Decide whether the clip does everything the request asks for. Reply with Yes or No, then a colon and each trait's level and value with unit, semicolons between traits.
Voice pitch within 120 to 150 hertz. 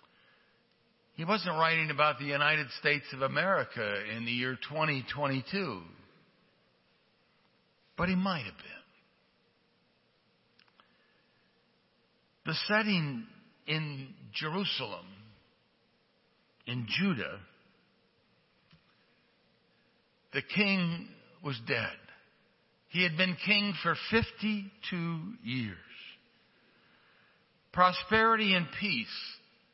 No: medium, 170 Hz